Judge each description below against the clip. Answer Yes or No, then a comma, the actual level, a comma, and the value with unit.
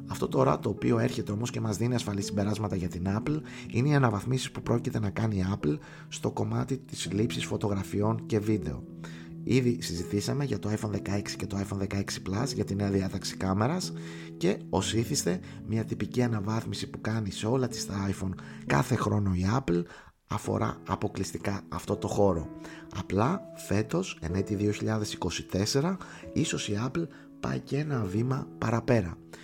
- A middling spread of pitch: Yes, average, 4.0 semitones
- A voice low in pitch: Yes, low, 105 Hz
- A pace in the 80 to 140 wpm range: No, average, 165 wpm